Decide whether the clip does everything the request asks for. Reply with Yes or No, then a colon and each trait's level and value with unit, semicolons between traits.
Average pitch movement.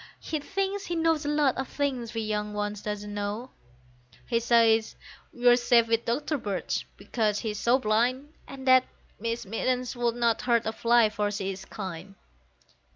Yes: average, 3.6 semitones